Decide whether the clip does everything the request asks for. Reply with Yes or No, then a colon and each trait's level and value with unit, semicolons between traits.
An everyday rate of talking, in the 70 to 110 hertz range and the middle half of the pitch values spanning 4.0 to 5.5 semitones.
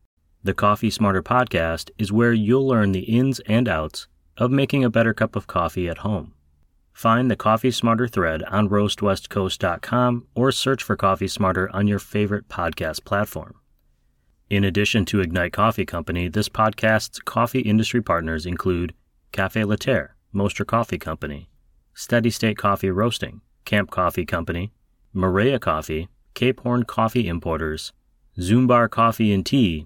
Yes: average, 145 wpm; low, 100 Hz; average, 4.8 semitones